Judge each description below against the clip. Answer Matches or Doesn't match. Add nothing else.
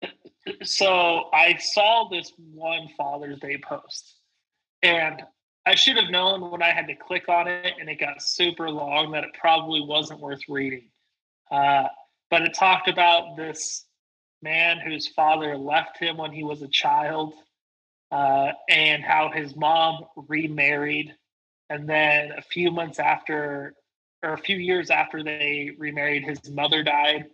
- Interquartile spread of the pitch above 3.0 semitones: Doesn't match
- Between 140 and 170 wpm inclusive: Matches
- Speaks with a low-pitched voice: Doesn't match